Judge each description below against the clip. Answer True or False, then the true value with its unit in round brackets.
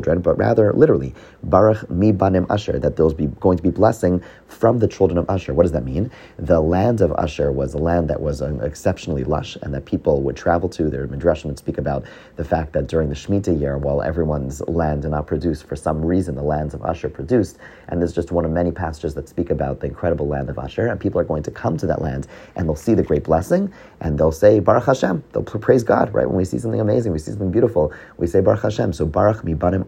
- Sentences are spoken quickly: True (245 wpm)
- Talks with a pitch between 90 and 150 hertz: False (80 Hz)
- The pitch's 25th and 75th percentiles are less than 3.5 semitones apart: False (3.8 semitones)